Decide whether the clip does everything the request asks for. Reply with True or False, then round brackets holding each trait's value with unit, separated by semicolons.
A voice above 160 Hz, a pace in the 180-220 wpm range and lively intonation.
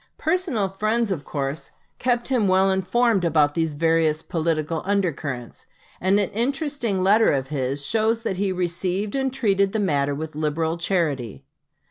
False (185 Hz; 155 wpm; 5.7 semitones)